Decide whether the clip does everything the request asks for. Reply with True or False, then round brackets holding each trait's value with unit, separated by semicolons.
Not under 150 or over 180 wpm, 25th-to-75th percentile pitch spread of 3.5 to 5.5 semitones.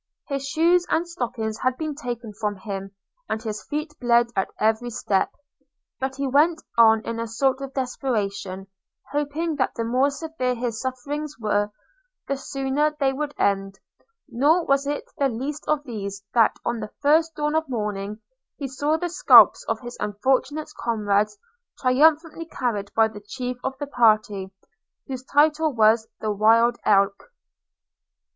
True (155 wpm; 5.0 semitones)